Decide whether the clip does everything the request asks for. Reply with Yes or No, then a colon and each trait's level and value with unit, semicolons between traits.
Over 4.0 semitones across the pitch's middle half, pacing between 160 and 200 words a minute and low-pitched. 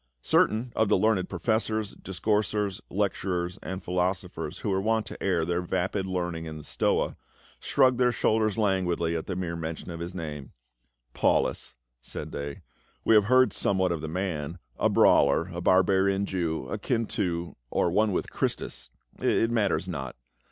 No: average, 3.7 semitones; average, 170 wpm; very low, 95 Hz